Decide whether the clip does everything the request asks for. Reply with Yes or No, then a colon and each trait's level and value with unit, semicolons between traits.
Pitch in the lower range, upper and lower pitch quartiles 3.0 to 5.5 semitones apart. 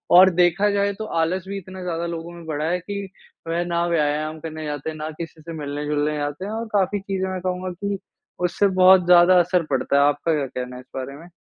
No: medium, 170 Hz; average, 3.5 semitones